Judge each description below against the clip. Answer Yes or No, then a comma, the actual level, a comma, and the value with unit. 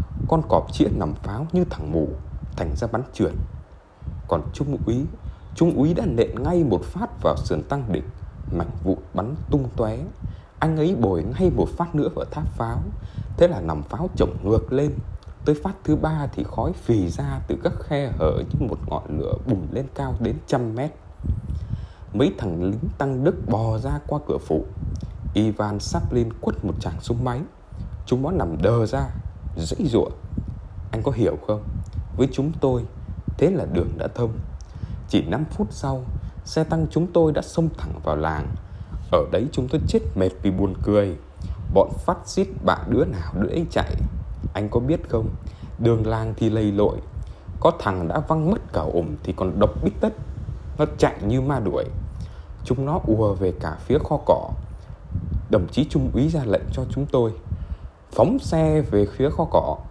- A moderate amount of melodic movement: No, wide, 6.8 semitones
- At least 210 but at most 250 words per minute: No, average, 185 wpm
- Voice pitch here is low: Yes, low, 105 Hz